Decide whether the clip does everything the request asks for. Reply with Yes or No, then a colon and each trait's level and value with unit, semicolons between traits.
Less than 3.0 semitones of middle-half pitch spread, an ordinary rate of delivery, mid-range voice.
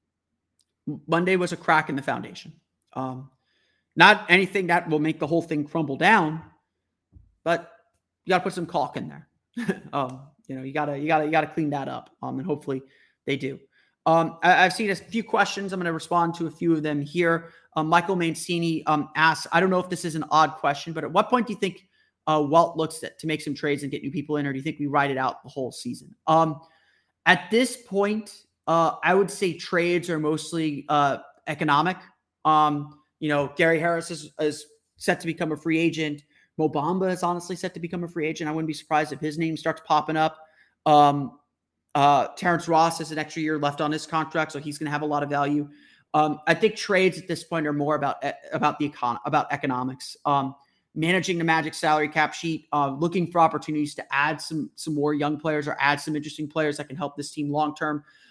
No: narrow, 2.5 semitones; fast, 225 wpm; medium, 155 Hz